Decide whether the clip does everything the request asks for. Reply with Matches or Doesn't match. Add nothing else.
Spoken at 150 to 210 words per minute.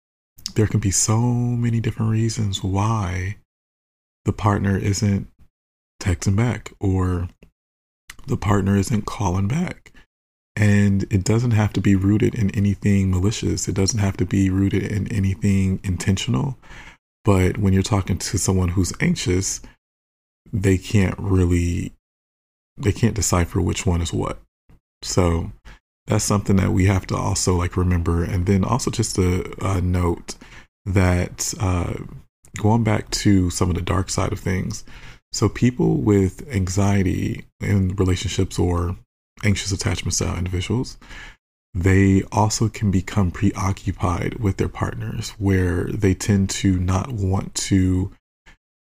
Doesn't match